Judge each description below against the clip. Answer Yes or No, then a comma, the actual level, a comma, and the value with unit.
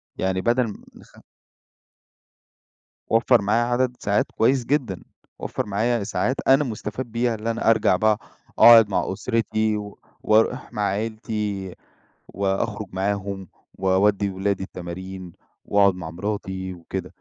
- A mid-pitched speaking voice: No, low, 105 Hz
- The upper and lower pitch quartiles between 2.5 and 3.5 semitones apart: Yes, average, 3.1 semitones